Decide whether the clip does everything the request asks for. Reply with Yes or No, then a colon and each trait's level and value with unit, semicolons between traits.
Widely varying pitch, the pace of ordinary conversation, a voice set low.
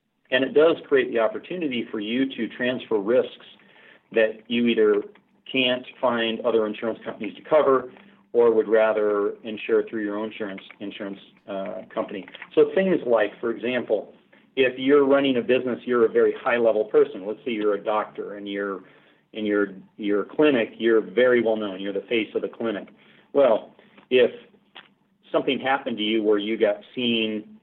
Yes: wide, 6.2 semitones; average, 170 wpm; low, 120 Hz